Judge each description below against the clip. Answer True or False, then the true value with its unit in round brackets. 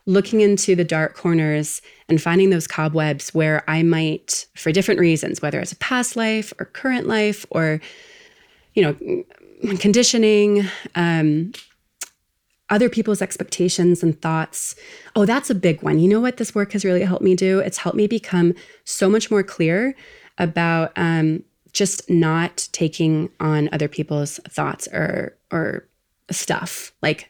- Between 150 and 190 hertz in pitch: True (185 Hz)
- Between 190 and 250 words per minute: False (145 wpm)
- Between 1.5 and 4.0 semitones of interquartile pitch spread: False (4.5 semitones)